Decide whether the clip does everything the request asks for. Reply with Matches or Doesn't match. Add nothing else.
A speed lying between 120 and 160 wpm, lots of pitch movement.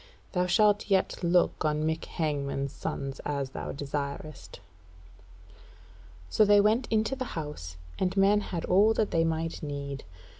Matches